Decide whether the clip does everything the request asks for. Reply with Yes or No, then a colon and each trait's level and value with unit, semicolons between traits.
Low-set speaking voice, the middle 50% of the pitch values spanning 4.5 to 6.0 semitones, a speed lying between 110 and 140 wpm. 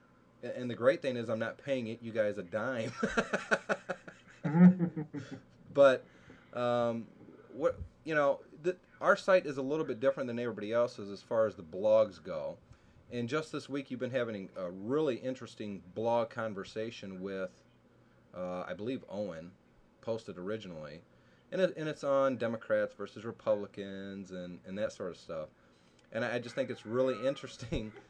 No: low, 115 Hz; average, 5.3 semitones; average, 160 wpm